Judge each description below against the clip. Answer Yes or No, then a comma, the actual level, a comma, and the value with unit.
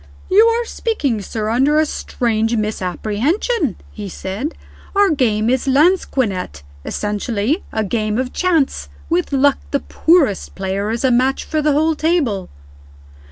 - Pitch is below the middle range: No, very high, 255 Hz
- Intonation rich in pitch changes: Yes, wide, 6.6 semitones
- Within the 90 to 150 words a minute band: Yes, average, 140 wpm